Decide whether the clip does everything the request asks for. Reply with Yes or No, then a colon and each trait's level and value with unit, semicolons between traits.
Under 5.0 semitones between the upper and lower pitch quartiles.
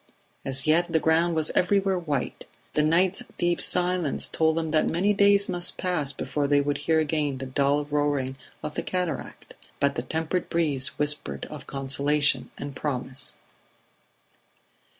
Yes: average, 3.5 semitones